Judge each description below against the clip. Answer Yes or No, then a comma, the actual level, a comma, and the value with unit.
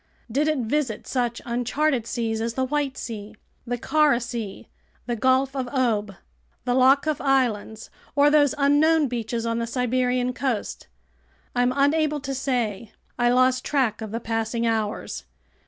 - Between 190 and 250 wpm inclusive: No, average, 150 wpm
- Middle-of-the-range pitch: No, very high, 250 Hz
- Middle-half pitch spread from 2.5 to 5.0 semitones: Yes, average, 3.1 semitones